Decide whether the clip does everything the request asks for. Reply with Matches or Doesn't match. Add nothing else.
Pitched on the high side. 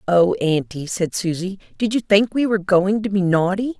Matches